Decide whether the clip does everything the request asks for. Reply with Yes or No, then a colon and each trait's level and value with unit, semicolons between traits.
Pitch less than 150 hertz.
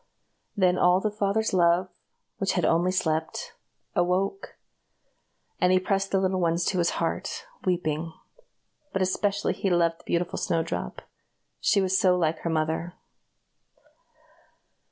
No: medium, 180 Hz